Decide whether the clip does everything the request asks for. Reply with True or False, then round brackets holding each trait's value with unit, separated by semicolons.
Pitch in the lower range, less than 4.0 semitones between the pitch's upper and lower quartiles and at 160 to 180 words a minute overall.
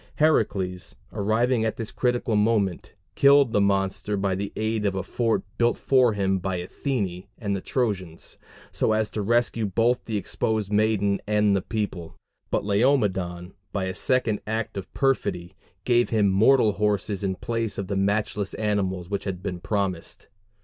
True (105 Hz; 2.8 semitones; 165 wpm)